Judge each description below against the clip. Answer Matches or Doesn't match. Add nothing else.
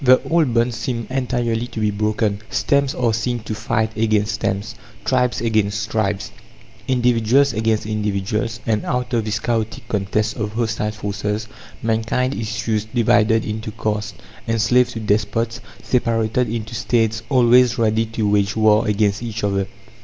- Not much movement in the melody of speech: Matches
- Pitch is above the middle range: Doesn't match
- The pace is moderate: Matches